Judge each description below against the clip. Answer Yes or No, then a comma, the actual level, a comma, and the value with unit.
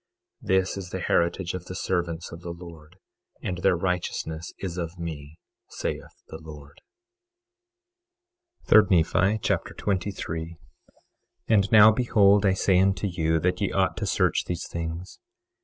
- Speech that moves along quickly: No, average, 145 wpm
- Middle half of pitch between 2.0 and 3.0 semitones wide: Yes, narrow, 2.6 semitones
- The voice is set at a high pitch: No, very low, 90 Hz